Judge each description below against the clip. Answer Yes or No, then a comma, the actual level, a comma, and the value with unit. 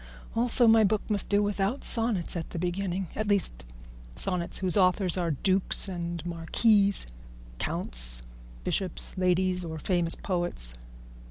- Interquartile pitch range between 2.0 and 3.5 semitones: Yes, average, 3.0 semitones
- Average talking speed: No, slow, 125 wpm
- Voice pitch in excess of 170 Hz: Yes, medium, 185 Hz